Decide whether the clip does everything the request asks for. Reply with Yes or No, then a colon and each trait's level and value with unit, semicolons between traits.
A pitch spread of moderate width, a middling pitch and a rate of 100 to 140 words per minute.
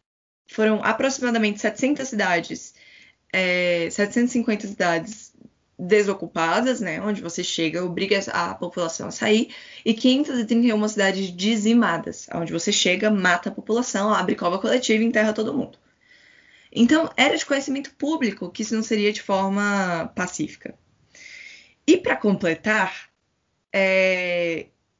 No: average, 4.2 semitones; high, 210 Hz; slow, 120 wpm